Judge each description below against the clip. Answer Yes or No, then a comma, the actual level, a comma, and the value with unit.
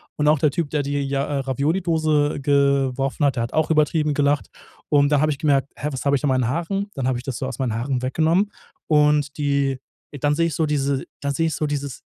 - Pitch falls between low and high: Yes, medium, 145 Hz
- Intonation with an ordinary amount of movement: No, narrow, 1.9 semitones